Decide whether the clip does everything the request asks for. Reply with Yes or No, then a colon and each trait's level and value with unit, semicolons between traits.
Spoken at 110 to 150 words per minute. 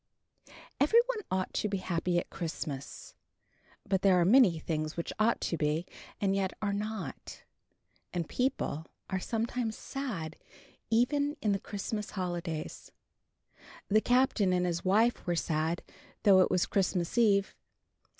Yes: average, 140 wpm